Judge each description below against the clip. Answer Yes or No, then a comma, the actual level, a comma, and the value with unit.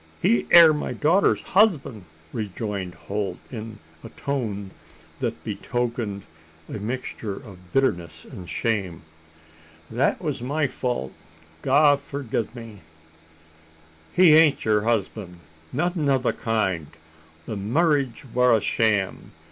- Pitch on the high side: No, low, 115 Hz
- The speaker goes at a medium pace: No, slow, 115 wpm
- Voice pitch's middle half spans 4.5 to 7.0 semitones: Yes, wide, 5.6 semitones